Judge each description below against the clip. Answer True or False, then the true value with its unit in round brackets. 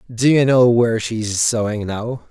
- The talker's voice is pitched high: False (115 Hz)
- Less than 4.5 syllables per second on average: True (4.2 syllables/s)